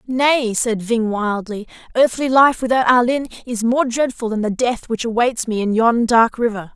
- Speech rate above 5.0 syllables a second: No, 4.6 syllables/s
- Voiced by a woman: Yes, female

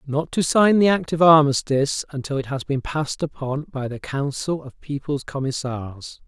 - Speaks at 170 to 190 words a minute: Yes, average, 180 wpm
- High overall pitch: No, medium, 145 Hz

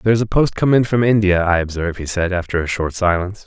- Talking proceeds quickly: Yes, fast, 275 wpm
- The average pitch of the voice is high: No, very low, 95 Hz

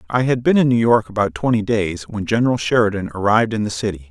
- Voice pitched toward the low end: Yes, low, 110 Hz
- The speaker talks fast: Yes, fast, 235 wpm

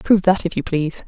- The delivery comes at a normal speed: No, fast, 280 wpm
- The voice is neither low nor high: Yes, medium, 180 Hz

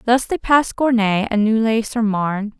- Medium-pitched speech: No, high, 225 Hz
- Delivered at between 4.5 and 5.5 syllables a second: Yes, 5.0 syllables/s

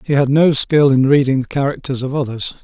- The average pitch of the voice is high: No, low, 135 Hz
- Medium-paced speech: No, fast, 225 wpm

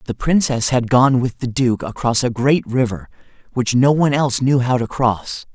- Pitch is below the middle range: Yes, low, 125 Hz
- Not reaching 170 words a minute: No, fast, 205 wpm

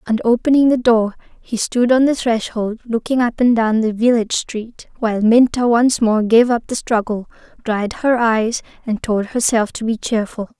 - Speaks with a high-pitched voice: Yes, high, 230 Hz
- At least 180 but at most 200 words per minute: Yes, average, 185 wpm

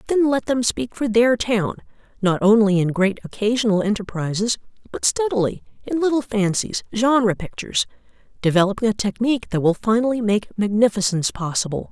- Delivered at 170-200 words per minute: No, average, 145 wpm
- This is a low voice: No, high, 215 Hz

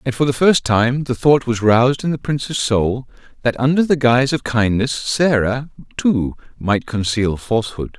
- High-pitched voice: No, low, 125 Hz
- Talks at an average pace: Yes, average, 180 wpm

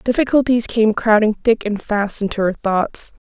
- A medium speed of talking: Yes, average, 165 wpm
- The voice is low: No, high, 225 Hz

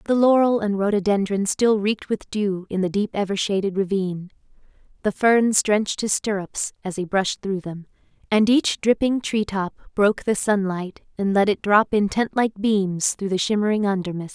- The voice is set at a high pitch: Yes, high, 200 Hz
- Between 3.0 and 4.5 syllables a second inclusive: No, 5.0 syllables/s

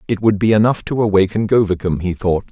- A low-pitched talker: Yes, low, 100 Hz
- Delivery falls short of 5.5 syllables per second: No, 6.1 syllables/s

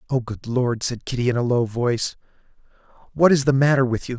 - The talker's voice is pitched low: Yes, low, 125 Hz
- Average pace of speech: No, fast, 215 wpm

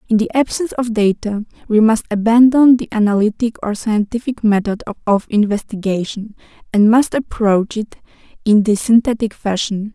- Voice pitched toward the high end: Yes, high, 220 Hz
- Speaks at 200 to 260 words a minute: No, average, 140 wpm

